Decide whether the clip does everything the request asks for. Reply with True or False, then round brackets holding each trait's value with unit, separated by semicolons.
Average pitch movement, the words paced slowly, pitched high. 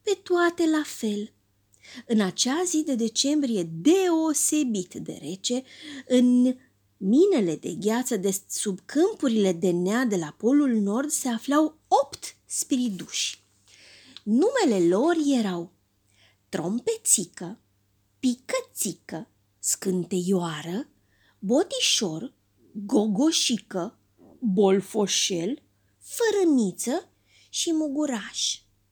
False (8.6 semitones; 85 wpm; 230 Hz)